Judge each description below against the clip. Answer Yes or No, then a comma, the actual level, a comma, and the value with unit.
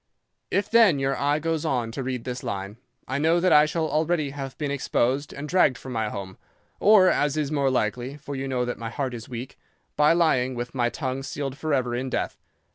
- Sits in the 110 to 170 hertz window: Yes, low, 135 Hz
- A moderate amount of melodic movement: Yes, average, 3.4 semitones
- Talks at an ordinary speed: No, fast, 215 wpm